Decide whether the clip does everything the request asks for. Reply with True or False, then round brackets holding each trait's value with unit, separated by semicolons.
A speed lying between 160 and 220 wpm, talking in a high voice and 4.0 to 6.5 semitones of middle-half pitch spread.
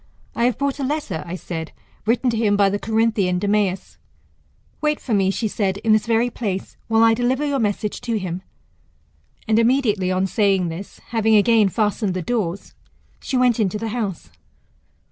False (180 wpm; 215 Hz; 3.3 semitones)